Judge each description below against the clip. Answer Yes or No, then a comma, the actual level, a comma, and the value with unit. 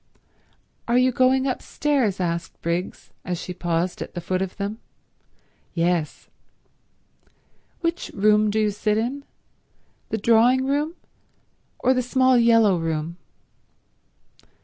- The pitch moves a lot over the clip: Yes, wide, 6.2 semitones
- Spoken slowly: Yes, slow, 120 wpm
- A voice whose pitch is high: Yes, high, 215 Hz